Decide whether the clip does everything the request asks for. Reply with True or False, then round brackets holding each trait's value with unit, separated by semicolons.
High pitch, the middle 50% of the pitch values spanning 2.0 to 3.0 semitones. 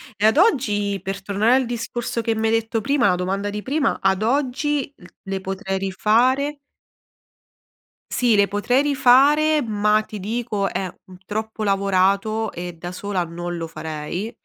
False (215 Hz; 4.1 semitones)